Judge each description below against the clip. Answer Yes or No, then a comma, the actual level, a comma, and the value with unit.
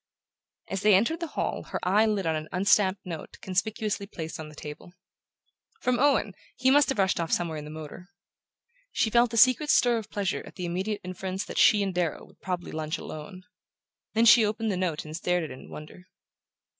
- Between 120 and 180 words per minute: No, fast, 205 wpm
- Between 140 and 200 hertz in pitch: Yes, high, 190 Hz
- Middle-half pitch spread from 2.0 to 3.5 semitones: No, average, 4.4 semitones